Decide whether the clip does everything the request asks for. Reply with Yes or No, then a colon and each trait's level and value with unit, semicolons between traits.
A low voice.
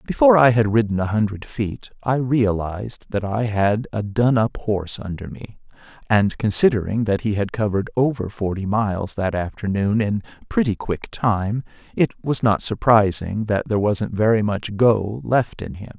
Yes: low, 110 Hz